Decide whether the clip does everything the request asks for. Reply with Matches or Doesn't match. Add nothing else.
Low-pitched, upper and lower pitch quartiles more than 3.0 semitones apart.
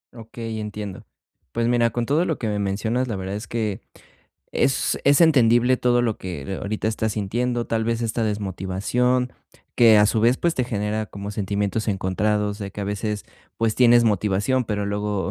Doesn't match